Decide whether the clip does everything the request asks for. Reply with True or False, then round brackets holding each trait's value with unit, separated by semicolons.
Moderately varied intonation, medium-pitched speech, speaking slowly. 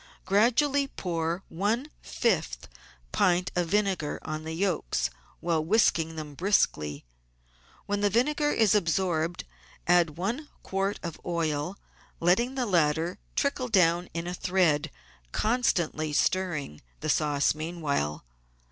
True (4.5 semitones; 175 Hz; 120 wpm)